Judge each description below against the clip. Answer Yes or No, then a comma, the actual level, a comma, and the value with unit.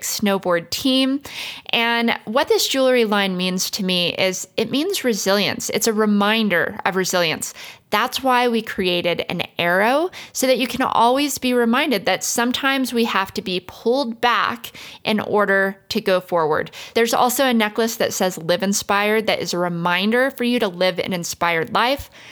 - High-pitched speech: Yes, high, 215 Hz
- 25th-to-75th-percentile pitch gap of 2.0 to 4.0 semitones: No, average, 4.8 semitones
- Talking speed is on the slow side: No, average, 170 wpm